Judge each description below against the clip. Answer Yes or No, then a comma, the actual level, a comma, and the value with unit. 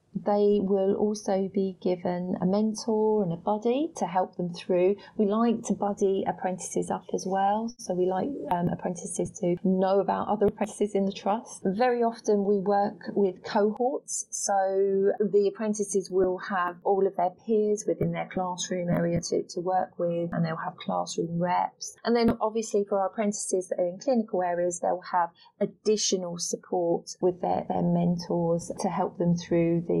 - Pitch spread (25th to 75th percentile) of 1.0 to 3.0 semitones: Yes, narrow, 2.4 semitones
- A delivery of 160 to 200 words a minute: Yes, average, 175 wpm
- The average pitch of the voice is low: No, high, 195 Hz